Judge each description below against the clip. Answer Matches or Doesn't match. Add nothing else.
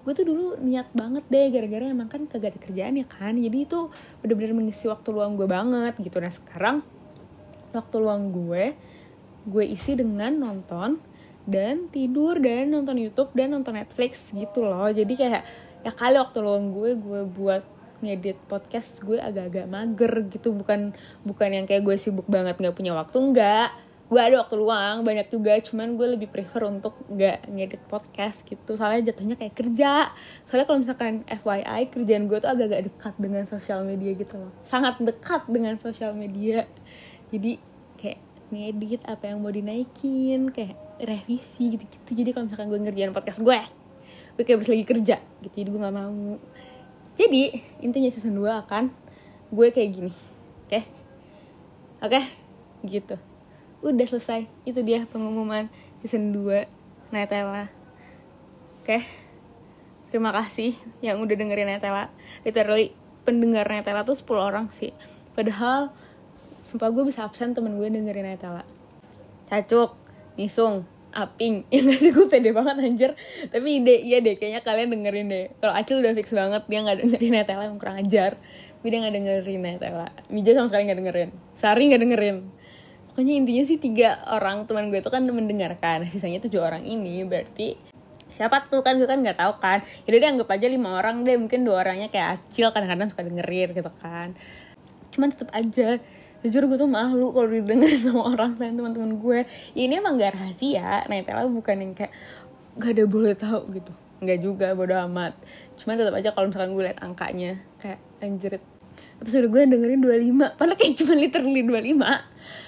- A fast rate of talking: Matches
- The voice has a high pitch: Matches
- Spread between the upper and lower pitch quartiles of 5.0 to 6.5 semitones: Doesn't match